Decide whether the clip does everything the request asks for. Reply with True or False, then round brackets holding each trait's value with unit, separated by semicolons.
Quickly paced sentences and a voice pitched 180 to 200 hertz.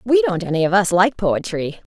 True (220 wpm; 185 Hz)